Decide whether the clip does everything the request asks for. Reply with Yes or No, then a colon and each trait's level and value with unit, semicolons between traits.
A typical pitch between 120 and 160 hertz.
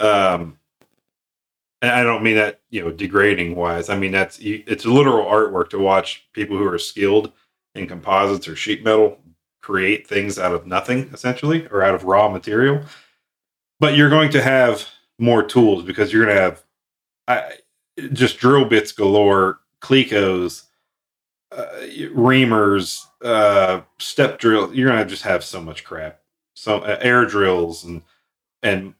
No: low, 105 Hz